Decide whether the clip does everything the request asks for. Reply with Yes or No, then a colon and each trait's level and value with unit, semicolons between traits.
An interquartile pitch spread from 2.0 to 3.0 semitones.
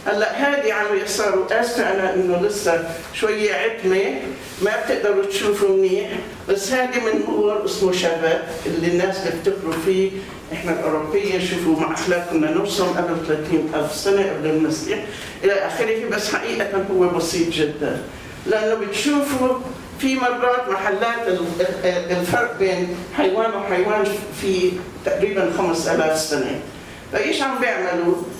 No: average, 3.7 semitones